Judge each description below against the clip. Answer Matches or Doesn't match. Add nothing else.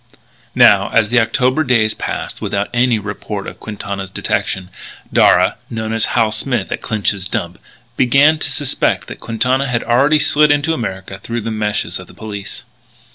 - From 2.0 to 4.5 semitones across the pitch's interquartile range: Matches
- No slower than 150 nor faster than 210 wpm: Matches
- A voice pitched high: Doesn't match